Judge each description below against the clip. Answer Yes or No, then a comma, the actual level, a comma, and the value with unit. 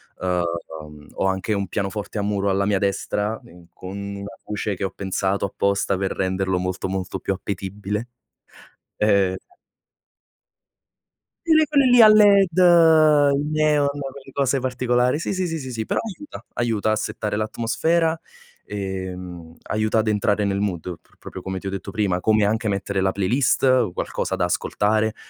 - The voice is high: No, low, 105 Hz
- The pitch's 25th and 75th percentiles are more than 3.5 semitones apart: Yes, wide, 5.5 semitones